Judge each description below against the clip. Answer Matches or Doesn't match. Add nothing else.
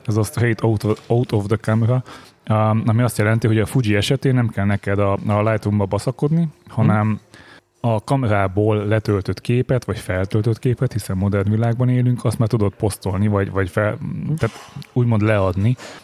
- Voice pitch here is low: Matches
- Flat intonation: Doesn't match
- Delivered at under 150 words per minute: Doesn't match